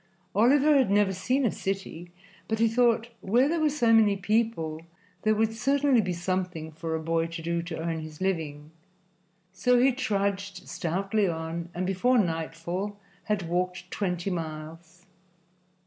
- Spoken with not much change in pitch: No, average, 5.1 semitones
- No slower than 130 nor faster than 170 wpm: Yes, average, 155 wpm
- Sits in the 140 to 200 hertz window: Yes, high, 190 Hz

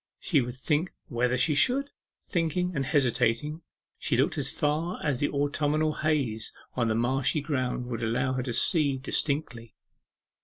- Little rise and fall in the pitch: No, average, 3.8 semitones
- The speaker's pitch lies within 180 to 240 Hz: No, medium, 140 Hz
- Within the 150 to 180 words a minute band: Yes, average, 155 wpm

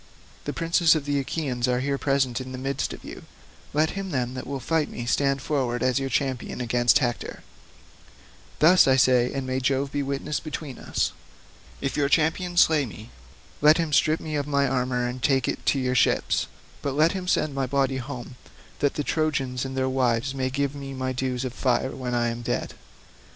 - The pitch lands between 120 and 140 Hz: Yes, low, 135 Hz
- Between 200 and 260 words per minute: Yes, fast, 205 wpm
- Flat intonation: Yes, narrow, 2.2 semitones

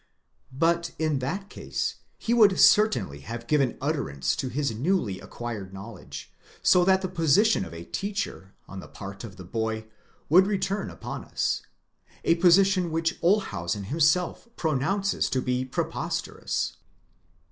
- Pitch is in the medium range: Yes, medium, 150 Hz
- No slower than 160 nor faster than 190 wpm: No, average, 140 wpm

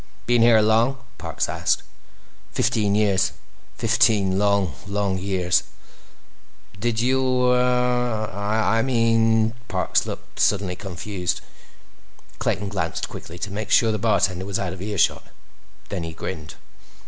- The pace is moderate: No, slow, 115 wpm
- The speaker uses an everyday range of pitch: Yes, average, 3.0 semitones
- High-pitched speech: No, low, 105 Hz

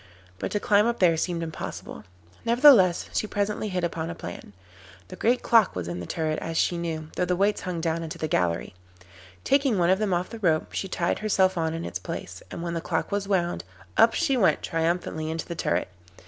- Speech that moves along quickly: Yes, fast, 215 wpm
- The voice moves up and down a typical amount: Yes, average, 4.0 semitones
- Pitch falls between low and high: Yes, medium, 175 Hz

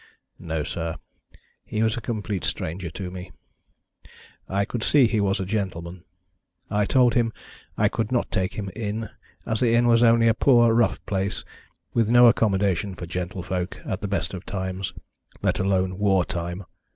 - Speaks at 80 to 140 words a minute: No, average, 170 wpm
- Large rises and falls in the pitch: No, average, 3.5 semitones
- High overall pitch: No, low, 100 Hz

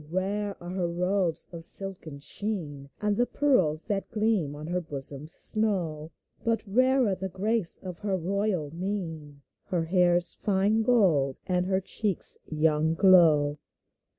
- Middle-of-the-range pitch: Yes, medium, 180 Hz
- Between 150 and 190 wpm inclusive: No, average, 140 wpm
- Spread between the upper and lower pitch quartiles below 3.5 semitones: No, average, 4.2 semitones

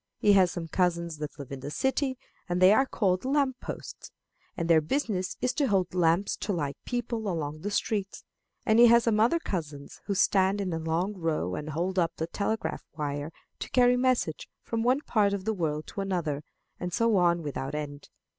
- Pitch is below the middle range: No, medium, 185 Hz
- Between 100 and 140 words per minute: No, average, 200 wpm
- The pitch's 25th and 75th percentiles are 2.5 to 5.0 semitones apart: No, wide, 5.4 semitones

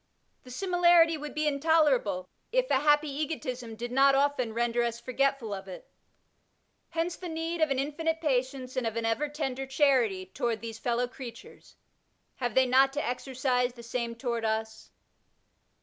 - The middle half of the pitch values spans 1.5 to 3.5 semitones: No, average, 4.0 semitones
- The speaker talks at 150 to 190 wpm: Yes, average, 165 wpm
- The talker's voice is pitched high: Yes, very high, 260 Hz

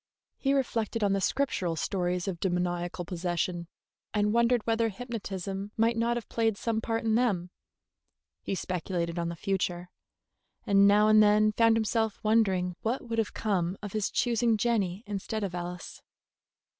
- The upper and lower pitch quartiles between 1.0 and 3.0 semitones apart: No, average, 4.0 semitones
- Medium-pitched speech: No, high, 205 Hz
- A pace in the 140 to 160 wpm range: Yes, average, 155 wpm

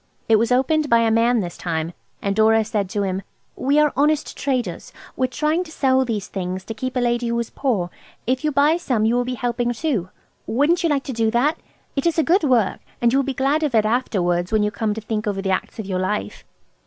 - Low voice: No, high, 235 Hz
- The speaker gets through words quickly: Yes, fast, 250 wpm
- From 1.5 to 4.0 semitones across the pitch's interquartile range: No, average, 4.7 semitones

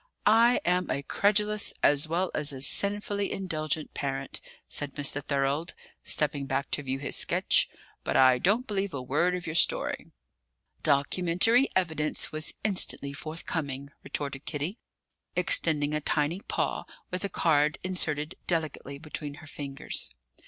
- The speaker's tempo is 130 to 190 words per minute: Yes, average, 140 wpm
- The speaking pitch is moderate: Yes, medium, 155 Hz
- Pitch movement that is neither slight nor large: Yes, average, 4.4 semitones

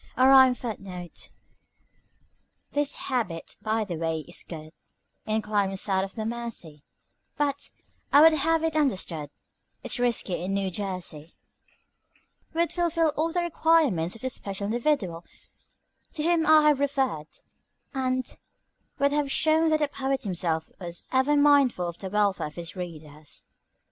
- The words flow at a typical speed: Yes, average, 150 wpm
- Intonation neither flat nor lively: No, wide, 8.3 semitones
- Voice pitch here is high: Yes, high, 230 Hz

